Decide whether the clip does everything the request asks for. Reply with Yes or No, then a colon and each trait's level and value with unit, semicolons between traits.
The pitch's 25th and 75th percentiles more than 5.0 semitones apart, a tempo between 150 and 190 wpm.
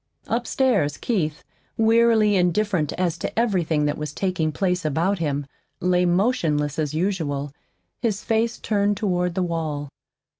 No: wide, 5.4 semitones; slow, 135 wpm